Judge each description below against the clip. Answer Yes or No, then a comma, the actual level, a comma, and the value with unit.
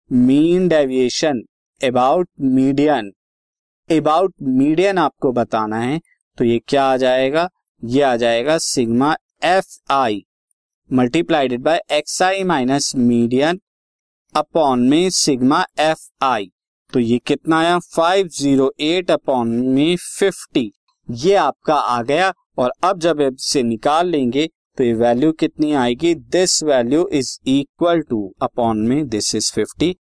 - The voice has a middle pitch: Yes, medium, 145 Hz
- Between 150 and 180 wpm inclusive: No, average, 130 wpm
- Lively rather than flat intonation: Yes, wide, 5.7 semitones